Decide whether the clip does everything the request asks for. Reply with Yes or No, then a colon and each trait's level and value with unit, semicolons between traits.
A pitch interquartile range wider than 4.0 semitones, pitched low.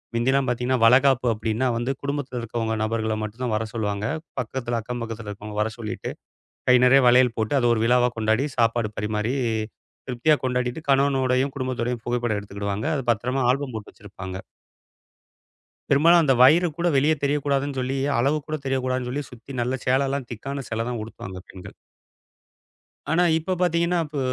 No: average, 3.5 semitones; low, 125 Hz